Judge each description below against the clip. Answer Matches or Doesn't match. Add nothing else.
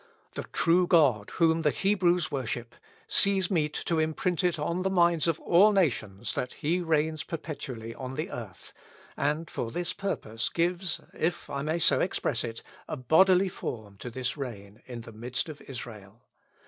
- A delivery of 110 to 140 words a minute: Doesn't match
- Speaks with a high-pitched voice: Doesn't match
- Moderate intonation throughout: Doesn't match